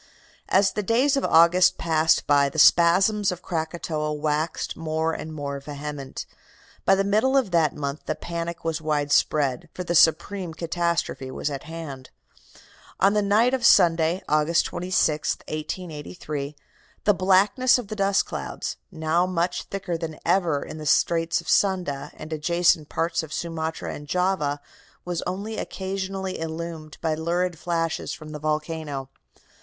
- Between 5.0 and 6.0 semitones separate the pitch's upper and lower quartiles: No, average, 3.2 semitones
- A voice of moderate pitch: Yes, medium, 165 Hz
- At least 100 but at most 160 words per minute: Yes, average, 150 wpm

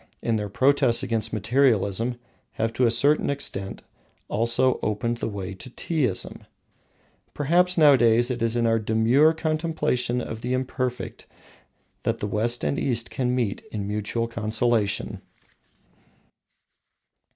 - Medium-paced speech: No, slow, 130 wpm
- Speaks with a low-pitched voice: Yes, low, 120 Hz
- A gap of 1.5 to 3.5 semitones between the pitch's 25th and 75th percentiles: Yes, average, 2.9 semitones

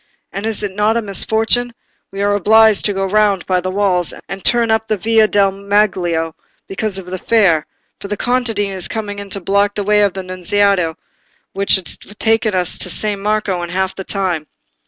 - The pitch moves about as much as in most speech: No, narrow, 2.2 semitones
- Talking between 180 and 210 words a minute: Yes, average, 200 wpm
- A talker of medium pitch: No, high, 200 Hz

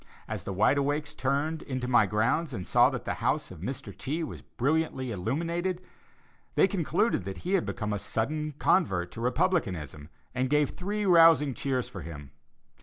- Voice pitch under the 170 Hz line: Yes, medium, 140 Hz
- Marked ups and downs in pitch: Yes, wide, 7.2 semitones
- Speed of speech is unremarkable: Yes, average, 175 wpm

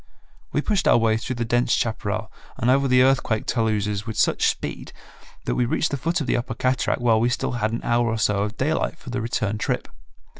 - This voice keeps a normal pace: No, fast, 225 wpm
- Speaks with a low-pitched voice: Yes, low, 120 Hz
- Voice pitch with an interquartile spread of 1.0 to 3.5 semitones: Yes, narrow, 2.5 semitones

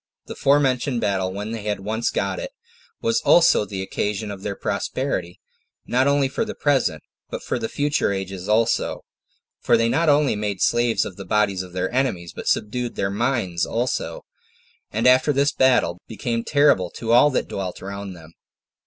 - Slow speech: No, average, 180 wpm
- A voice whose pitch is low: Yes, low, 110 Hz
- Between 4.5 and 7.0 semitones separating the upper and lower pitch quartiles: Yes, average, 5.2 semitones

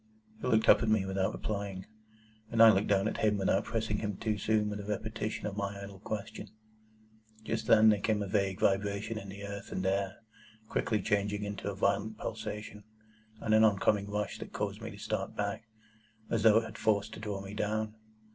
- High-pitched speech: No, low, 105 Hz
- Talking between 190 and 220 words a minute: Yes, fast, 205 wpm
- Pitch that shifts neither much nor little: No, narrow, 1.5 semitones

